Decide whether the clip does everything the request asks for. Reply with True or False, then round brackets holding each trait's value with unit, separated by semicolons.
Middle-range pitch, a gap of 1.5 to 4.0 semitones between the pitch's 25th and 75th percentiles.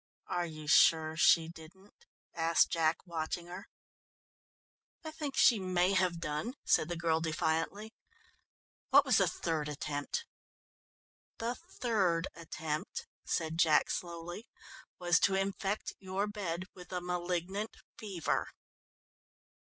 True (175 Hz; 3.0 semitones)